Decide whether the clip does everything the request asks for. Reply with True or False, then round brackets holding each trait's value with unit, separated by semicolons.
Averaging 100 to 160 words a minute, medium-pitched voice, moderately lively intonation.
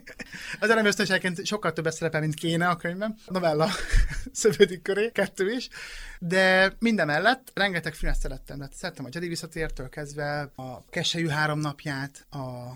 True (155 wpm; 170 Hz; 4.7 semitones)